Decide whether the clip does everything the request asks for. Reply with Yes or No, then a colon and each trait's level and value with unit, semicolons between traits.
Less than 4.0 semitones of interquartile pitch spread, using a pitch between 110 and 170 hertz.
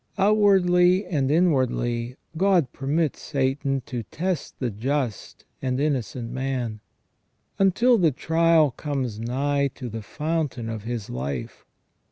No: wide, 5.6 semitones; low, 135 Hz